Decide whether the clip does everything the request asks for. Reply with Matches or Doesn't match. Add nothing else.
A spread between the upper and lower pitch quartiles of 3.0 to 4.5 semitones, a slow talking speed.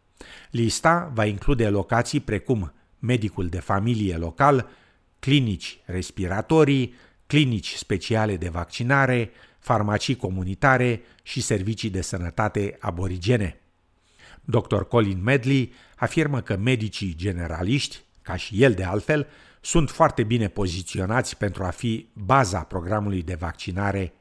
Doesn't match